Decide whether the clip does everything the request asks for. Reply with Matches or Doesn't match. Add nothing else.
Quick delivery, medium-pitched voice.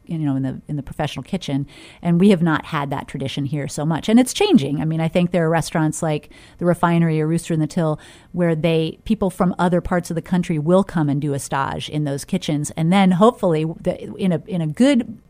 Matches